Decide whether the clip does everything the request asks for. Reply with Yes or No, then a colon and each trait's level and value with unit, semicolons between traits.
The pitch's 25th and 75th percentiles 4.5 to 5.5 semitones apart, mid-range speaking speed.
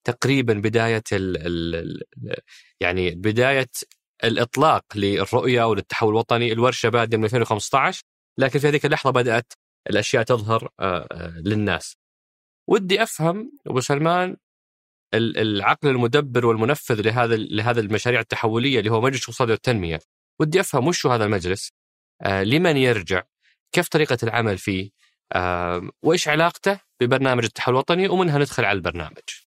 Yes: average, 5.1 semitones; average, 120 wpm